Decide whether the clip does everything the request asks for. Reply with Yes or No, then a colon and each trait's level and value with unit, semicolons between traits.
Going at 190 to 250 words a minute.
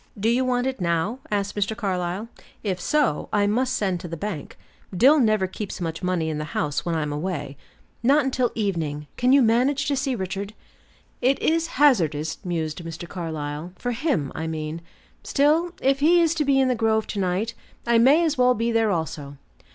Yes: average, 195 wpm